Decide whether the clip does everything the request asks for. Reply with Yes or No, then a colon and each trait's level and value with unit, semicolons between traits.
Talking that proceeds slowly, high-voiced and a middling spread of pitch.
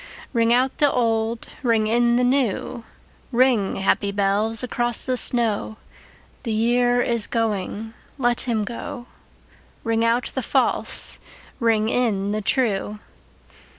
No: slow, 125 wpm; high, 230 Hz; narrow, 2.2 semitones